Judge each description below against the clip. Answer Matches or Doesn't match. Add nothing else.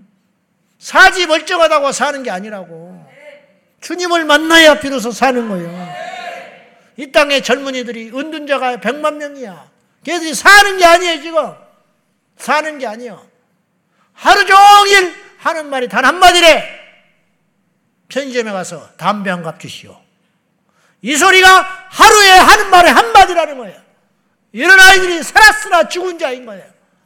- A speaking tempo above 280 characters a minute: Doesn't match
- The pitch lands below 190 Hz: Doesn't match